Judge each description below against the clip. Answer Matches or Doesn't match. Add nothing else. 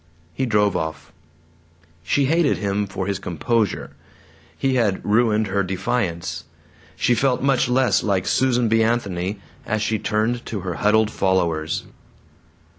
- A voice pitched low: Matches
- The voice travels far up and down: Doesn't match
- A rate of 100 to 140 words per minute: Matches